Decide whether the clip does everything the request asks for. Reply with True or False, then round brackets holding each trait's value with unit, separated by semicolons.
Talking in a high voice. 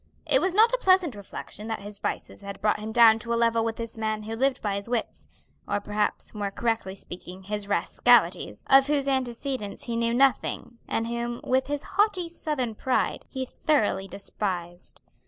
True (230 Hz)